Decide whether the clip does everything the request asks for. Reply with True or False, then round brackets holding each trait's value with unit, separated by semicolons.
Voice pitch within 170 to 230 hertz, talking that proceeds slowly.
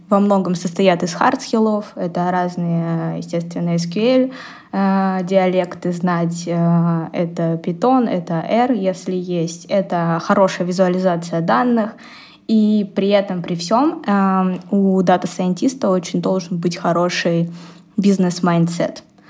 True (185 Hz; 105 wpm)